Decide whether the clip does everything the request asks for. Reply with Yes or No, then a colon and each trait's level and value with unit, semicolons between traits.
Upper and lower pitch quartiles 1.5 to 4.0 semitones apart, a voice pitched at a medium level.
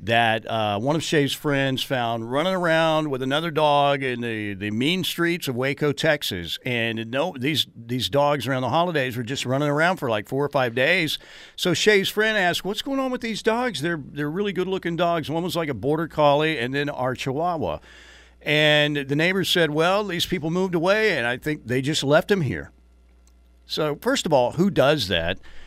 No: average, 5.1 semitones; medium, 145 Hz